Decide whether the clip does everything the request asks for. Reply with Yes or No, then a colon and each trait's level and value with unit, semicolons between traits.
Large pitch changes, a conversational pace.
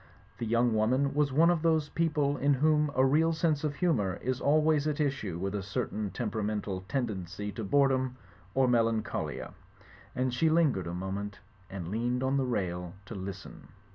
Yes: wide, 6.2 semitones; average, 170 wpm